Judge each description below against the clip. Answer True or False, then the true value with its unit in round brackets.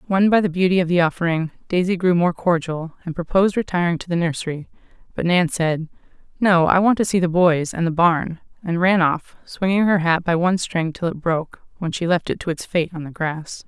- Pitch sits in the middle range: True (175 Hz)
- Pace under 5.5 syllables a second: False (5.6 syllables/s)